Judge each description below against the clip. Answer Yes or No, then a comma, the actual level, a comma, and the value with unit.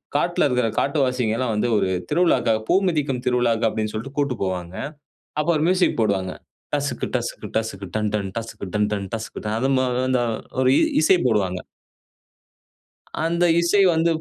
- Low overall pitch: Yes, low, 120 Hz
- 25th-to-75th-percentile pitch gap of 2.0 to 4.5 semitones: No, average, 5.1 semitones